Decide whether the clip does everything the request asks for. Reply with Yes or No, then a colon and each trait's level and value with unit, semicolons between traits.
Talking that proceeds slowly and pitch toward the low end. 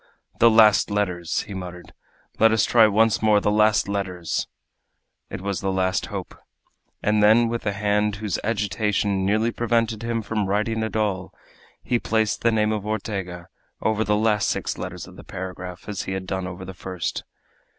No: average, 180 wpm; low, 105 Hz